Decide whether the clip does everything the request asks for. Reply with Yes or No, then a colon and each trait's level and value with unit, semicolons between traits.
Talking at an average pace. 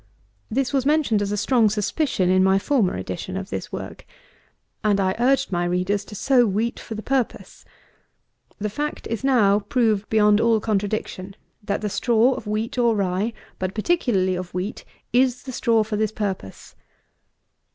Yes: average, 170 wpm